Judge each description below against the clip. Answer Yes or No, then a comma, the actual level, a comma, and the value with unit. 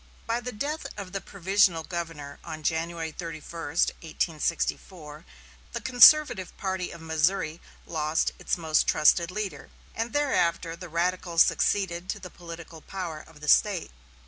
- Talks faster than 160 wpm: No, average, 140 wpm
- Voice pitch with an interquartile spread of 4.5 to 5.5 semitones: No, average, 3.2 semitones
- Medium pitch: Yes, medium, 170 Hz